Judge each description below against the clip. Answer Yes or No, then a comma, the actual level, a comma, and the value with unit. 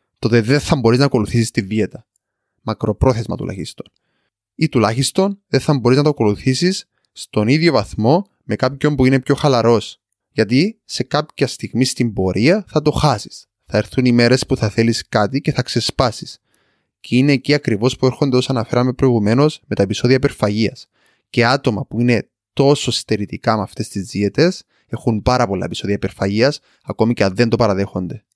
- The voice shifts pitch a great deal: No, average, 4.1 semitones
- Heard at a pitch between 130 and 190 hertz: No, low, 120 Hz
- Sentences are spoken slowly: No, fast, 170 wpm